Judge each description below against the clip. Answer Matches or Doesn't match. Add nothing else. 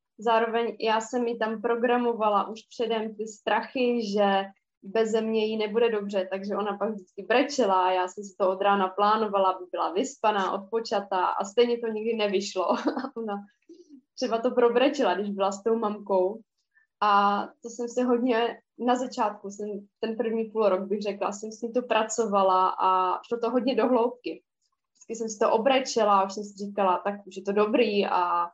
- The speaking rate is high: Matches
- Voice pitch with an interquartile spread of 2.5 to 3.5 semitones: Matches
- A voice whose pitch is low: Doesn't match